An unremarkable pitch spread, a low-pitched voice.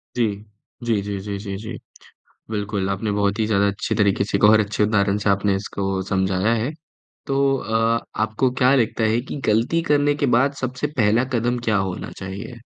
Yes: average, 3.3 semitones; low, 110 Hz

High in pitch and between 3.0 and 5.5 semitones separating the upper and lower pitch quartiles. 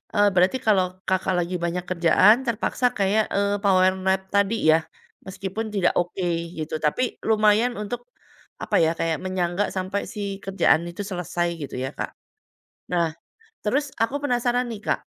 Yes: high, 195 Hz; average, 3.4 semitones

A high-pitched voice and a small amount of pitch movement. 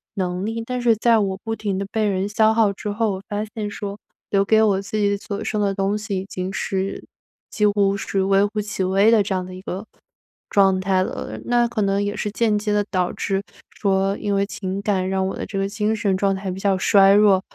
Yes: high, 200 Hz; narrow, 1.6 semitones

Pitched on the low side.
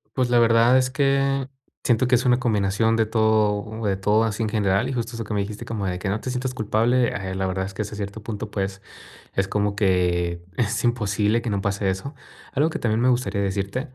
Yes: low, 110 Hz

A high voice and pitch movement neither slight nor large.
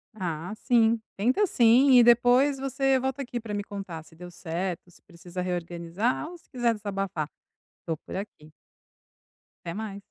No: high, 205 Hz; wide, 5.7 semitones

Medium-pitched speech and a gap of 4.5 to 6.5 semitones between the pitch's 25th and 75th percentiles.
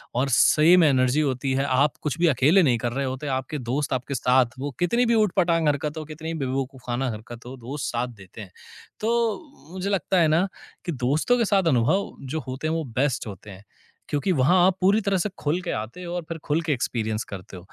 Yes: medium, 145 Hz; average, 5.0 semitones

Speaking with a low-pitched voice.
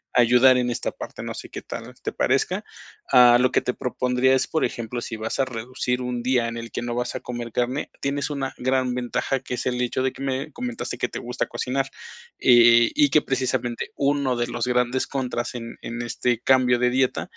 Yes: low, 125 Hz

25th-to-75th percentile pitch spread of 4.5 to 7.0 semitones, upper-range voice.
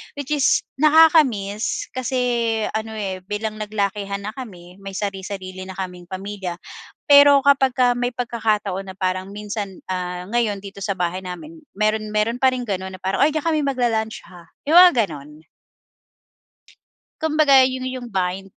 Yes: average, 5.2 semitones; high, 210 Hz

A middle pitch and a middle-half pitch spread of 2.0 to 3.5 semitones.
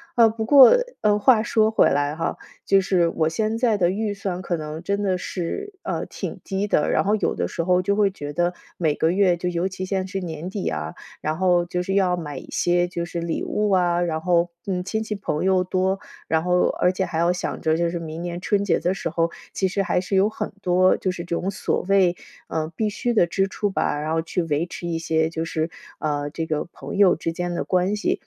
Yes: medium, 180 Hz; average, 2.8 semitones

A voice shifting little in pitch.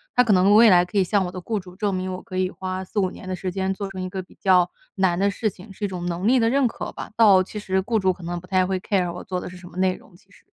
Yes: narrow, 1.8 semitones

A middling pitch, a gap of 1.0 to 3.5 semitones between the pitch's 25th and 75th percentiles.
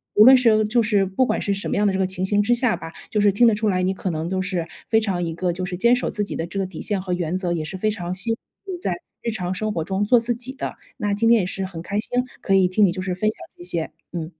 No: high, 195 Hz; average, 3.0 semitones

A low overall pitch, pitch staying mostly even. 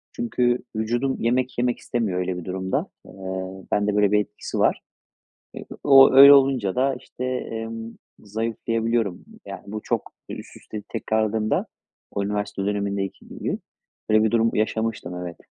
No: low, 110 Hz; average, 3.0 semitones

